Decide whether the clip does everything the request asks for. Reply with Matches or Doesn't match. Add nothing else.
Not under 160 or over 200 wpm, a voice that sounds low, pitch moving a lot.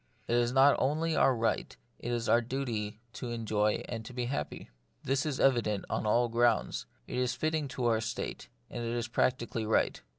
Doesn't match